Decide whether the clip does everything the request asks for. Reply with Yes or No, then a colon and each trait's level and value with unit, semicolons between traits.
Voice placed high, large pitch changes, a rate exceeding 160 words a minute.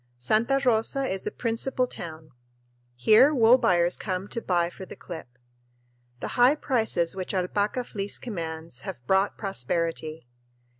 No: high, 195 Hz; wide, 5.7 semitones; average, 140 wpm